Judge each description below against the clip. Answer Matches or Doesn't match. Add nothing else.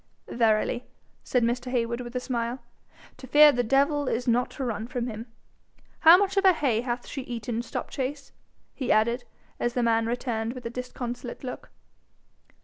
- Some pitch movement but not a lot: Doesn't match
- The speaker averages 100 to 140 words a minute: Doesn't match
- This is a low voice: Doesn't match